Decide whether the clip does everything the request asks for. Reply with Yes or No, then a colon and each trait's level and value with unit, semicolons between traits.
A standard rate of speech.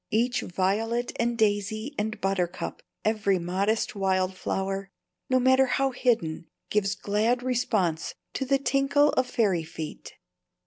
No: slow, 130 wpm